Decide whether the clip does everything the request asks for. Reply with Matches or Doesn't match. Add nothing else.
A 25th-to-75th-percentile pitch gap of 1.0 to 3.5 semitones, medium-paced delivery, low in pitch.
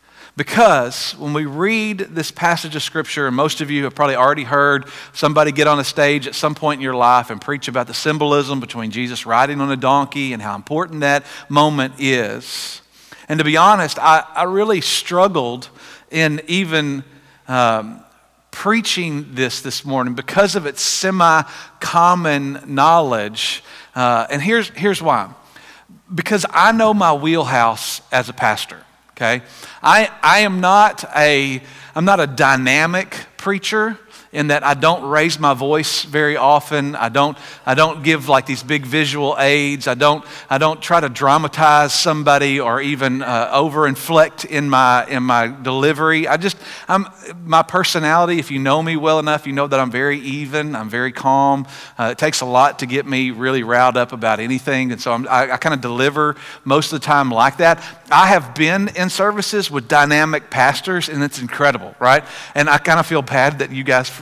Doesn't match